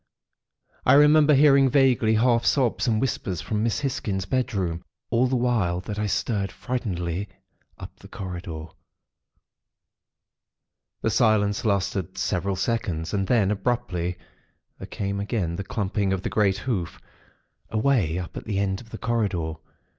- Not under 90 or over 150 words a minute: Yes, average, 140 wpm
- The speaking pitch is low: Yes, low, 105 Hz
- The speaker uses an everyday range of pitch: Yes, average, 4.2 semitones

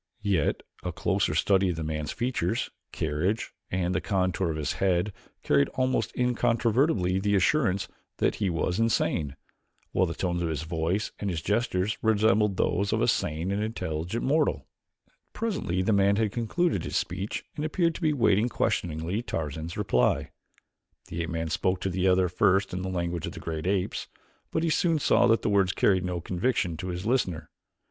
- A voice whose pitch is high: No, very low, 95 Hz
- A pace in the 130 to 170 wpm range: No, average, 180 wpm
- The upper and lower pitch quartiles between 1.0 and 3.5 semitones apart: No, average, 4.4 semitones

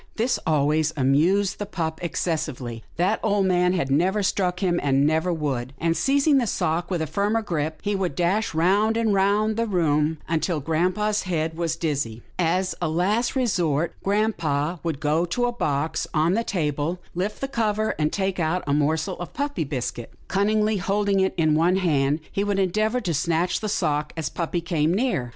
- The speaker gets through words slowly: No, average, 185 wpm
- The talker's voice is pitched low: No, medium, 175 Hz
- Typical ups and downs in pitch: Yes, average, 4.6 semitones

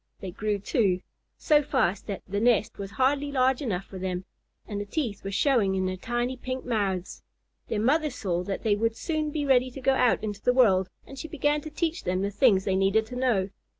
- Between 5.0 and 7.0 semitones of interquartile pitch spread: Yes, average, 5.3 semitones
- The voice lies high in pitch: Yes, high, 225 Hz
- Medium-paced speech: No, fast, 220 wpm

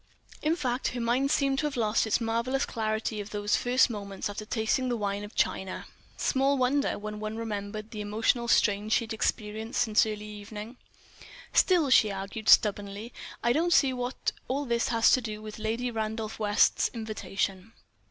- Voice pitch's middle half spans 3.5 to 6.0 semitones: No, average, 2.8 semitones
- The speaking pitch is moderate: No, high, 220 Hz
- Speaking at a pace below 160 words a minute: No, average, 175 wpm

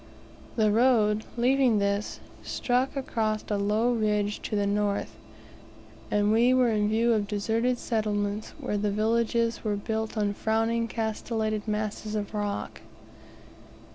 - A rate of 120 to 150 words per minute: Yes, slow, 135 wpm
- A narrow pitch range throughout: Yes, narrow, 1.8 semitones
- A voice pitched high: Yes, high, 215 Hz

